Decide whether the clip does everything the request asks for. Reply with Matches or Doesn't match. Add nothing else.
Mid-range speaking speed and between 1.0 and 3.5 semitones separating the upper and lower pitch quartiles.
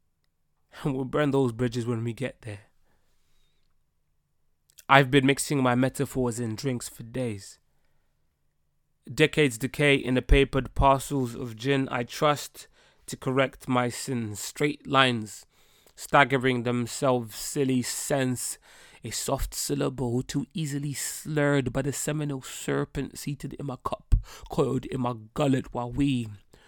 Doesn't match